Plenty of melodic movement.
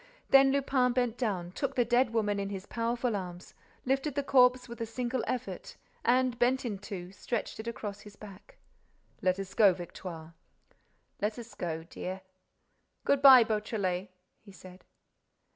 No: average, 4.5 semitones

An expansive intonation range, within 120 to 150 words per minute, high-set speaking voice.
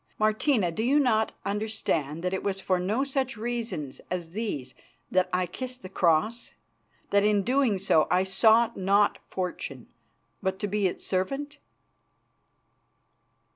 No: average, 4.2 semitones; average, 140 wpm; high, 205 Hz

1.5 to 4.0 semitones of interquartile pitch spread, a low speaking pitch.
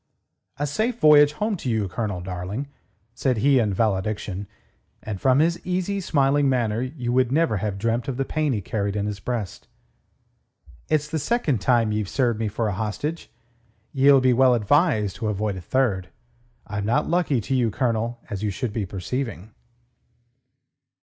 No: average, 5.2 semitones; low, 120 Hz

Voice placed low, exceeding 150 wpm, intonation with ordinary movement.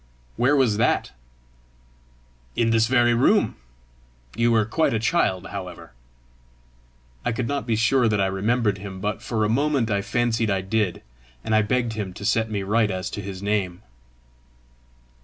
Yes: low, 110 Hz; average, 165 wpm; average, 3.0 semitones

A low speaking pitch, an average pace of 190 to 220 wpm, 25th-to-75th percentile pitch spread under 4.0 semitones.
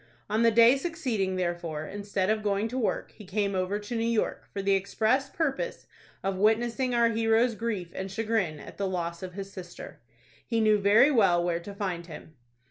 No: high, 205 Hz; average, 195 wpm; average, 3.5 semitones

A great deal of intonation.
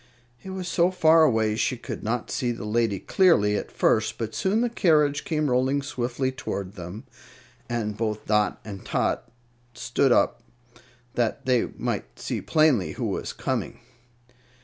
Yes: wide, 6.0 semitones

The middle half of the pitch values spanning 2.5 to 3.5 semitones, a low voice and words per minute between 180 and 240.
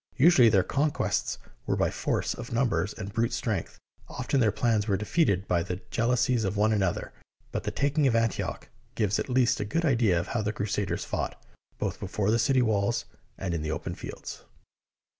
No: average, 3.9 semitones; low, 110 Hz; average, 195 wpm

